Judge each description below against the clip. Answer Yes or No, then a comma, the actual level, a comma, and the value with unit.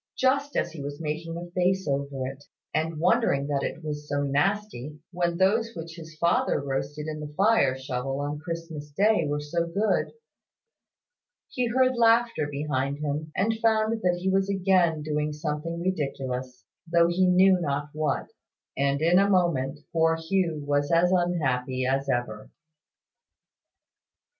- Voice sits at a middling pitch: Yes, medium, 160 Hz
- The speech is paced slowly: No, average, 155 wpm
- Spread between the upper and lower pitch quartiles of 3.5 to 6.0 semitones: Yes, average, 4.3 semitones